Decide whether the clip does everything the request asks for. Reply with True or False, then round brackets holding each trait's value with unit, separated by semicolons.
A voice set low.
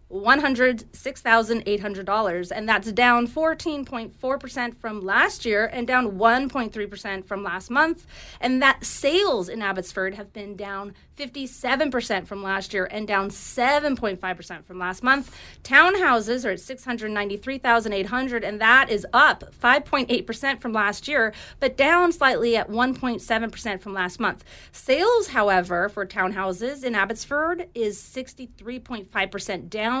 False (230 Hz)